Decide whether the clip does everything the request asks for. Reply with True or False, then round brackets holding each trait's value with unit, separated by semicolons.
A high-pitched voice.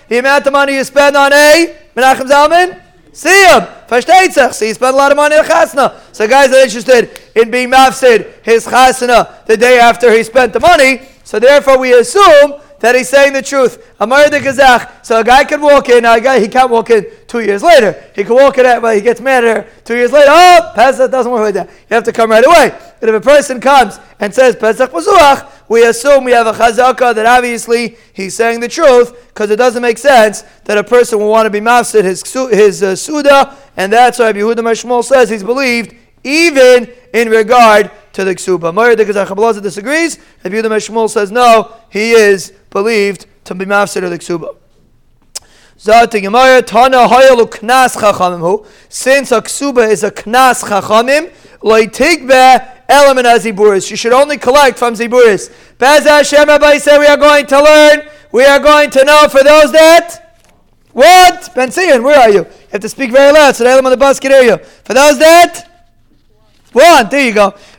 True (255 Hz)